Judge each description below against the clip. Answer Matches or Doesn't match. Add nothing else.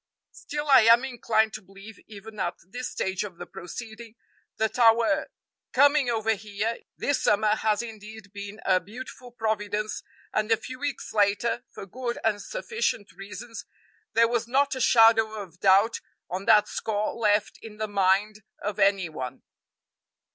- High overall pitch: Matches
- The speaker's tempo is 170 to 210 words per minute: Doesn't match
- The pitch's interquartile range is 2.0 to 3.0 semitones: Matches